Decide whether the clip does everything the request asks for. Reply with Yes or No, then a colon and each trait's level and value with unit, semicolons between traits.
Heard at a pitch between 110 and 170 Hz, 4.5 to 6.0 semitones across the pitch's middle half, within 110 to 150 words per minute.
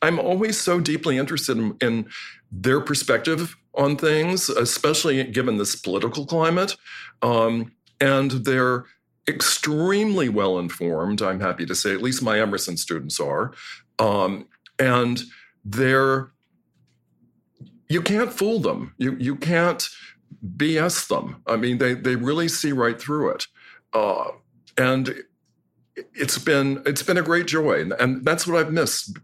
Yes: medium, 140 Hz; average, 4.9 semitones; average, 140 wpm